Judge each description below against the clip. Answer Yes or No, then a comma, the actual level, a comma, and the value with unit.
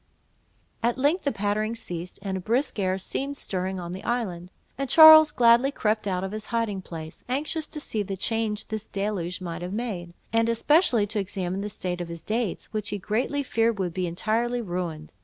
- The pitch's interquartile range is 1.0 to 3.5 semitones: No, average, 4.4 semitones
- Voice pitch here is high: Yes, high, 210 Hz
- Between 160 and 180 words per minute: No, average, 195 wpm